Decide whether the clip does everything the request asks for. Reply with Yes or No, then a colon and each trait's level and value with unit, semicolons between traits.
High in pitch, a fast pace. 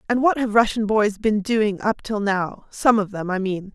Yes: high, 210 Hz; fast, 240 wpm